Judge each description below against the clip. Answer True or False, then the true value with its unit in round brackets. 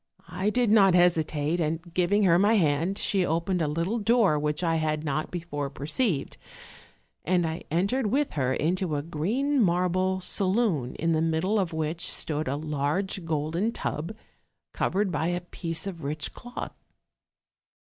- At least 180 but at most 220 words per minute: False (160 wpm)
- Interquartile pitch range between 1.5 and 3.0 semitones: False (3.9 semitones)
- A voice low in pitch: False (170 Hz)